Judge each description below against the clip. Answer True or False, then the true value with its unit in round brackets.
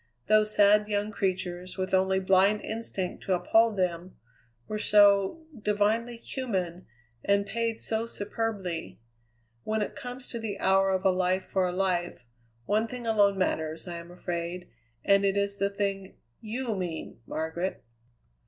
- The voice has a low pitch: False (200 Hz)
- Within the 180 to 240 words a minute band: False (150 wpm)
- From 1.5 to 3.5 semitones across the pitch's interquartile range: True (2.6 semitones)